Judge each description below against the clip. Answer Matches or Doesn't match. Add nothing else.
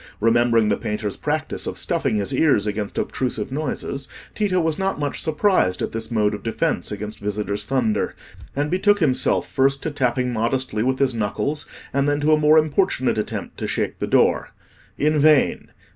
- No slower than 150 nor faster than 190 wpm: Matches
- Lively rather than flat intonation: Matches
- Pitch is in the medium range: Doesn't match